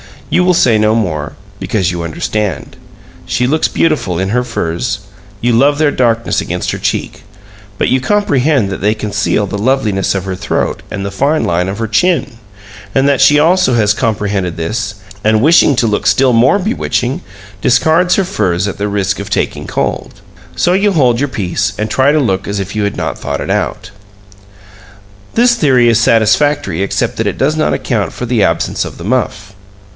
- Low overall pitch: Yes, low, 115 Hz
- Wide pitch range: Yes, wide, 5.9 semitones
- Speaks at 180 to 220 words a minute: Yes, average, 190 wpm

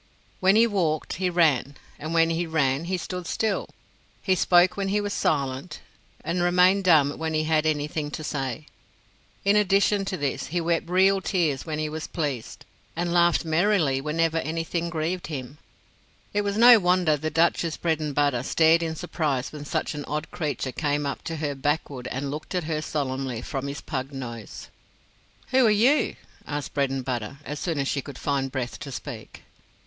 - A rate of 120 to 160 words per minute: No, average, 180 wpm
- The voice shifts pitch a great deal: No, average, 3.8 semitones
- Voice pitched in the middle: Yes, medium, 155 Hz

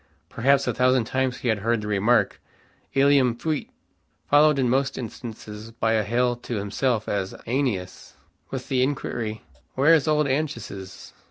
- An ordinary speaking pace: Yes, average, 155 wpm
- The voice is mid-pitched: No, low, 125 Hz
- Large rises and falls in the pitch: No, average, 3.8 semitones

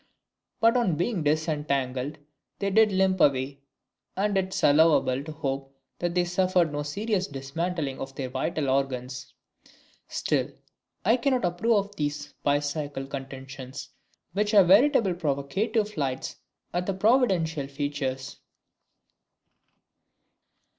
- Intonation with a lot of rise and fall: Yes, wide, 5.7 semitones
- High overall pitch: No, medium, 155 Hz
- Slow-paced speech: Yes, slow, 120 wpm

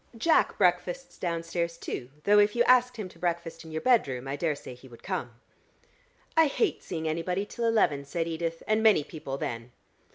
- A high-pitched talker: No, medium, 170 Hz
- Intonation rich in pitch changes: Yes, wide, 6.2 semitones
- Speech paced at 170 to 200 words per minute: Yes, average, 185 wpm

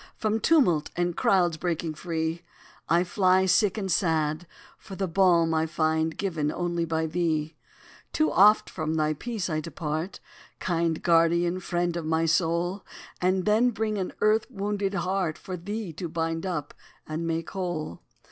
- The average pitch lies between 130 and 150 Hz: No, medium, 175 Hz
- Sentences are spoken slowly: No, average, 155 wpm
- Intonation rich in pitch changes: No, average, 2.9 semitones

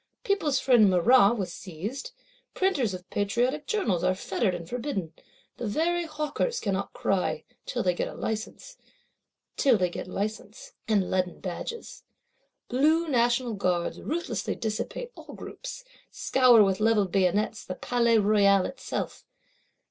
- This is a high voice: Yes, high, 220 Hz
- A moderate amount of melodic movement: No, wide, 6.1 semitones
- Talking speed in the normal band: No, slow, 120 wpm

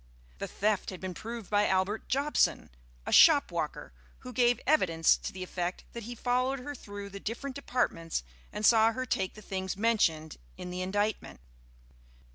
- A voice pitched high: Yes, high, 210 Hz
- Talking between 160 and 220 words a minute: Yes, average, 165 wpm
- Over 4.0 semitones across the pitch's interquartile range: Yes, average, 4.5 semitones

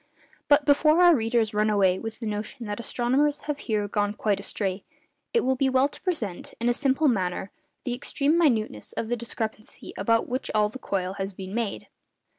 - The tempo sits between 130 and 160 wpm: No, average, 195 wpm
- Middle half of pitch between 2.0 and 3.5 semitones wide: No, average, 4.5 semitones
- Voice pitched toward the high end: Yes, high, 230 Hz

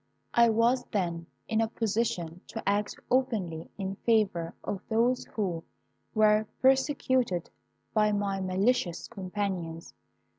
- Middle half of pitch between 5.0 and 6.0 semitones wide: No, average, 3.9 semitones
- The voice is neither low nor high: No, high, 210 Hz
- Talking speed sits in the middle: No, slow, 115 wpm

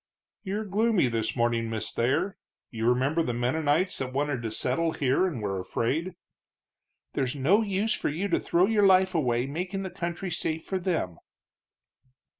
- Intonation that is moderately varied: No, wide, 7.3 semitones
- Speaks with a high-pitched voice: No, medium, 155 Hz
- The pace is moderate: Yes, average, 165 wpm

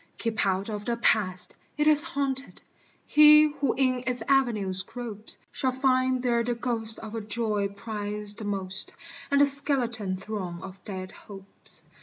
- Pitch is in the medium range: No, high, 225 Hz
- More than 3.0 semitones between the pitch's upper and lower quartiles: Yes, average, 4.3 semitones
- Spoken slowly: No, average, 160 wpm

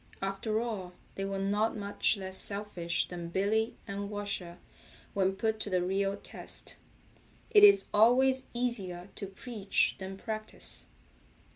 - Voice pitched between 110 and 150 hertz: No, high, 200 Hz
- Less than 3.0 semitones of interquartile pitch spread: Yes, narrow, 2.4 semitones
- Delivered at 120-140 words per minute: Yes, slow, 135 wpm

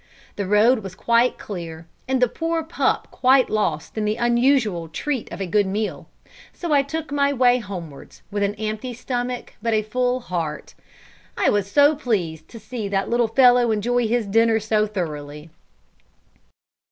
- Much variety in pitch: No, average, 4.0 semitones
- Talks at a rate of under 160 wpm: No, average, 165 wpm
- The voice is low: No, high, 220 Hz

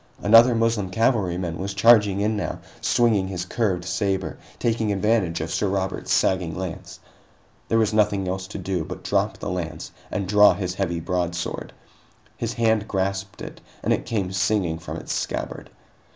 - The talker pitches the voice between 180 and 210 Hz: No, very low, 95 Hz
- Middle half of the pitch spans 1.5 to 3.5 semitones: Yes, average, 2.8 semitones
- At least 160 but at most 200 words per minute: Yes, average, 165 wpm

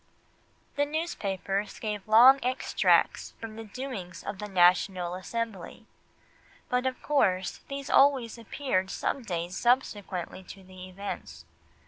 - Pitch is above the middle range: Yes, high, 210 Hz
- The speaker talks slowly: Yes, slow, 120 wpm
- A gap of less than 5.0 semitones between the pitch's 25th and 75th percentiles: No, wide, 5.4 semitones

